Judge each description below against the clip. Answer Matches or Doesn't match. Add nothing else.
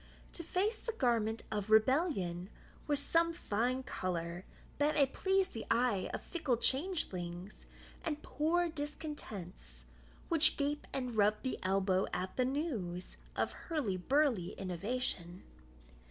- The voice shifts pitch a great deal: Matches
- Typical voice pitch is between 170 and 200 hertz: Doesn't match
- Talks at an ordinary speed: Doesn't match